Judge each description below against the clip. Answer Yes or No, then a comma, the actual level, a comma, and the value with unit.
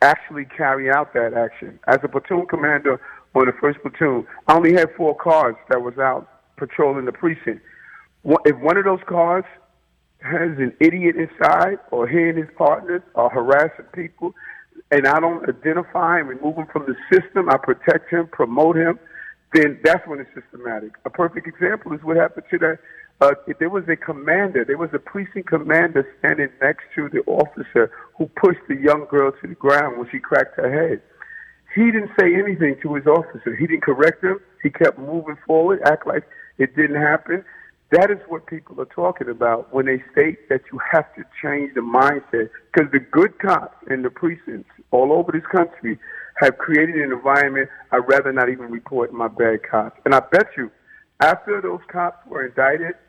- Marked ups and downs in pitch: No, average, 3.9 semitones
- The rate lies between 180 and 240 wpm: Yes, average, 185 wpm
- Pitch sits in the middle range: Yes, medium, 155 Hz